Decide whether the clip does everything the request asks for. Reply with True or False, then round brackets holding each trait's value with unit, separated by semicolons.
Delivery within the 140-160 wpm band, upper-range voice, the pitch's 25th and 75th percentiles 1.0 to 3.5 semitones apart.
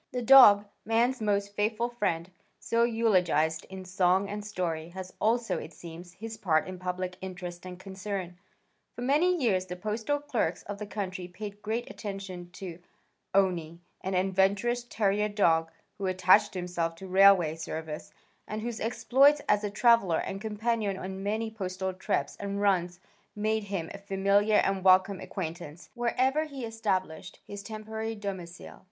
True (155 wpm; 200 Hz; 3.2 semitones)